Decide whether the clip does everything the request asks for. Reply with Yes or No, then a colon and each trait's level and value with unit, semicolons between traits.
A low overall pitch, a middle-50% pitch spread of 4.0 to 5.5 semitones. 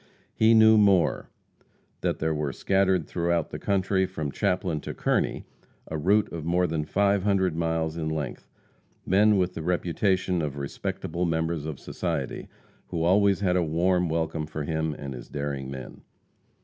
No: very low, 85 Hz; average, 3.3 semitones